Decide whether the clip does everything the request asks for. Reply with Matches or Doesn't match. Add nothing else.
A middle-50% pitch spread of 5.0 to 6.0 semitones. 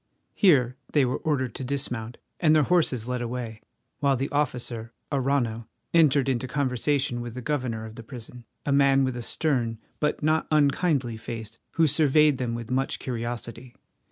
Doesn't match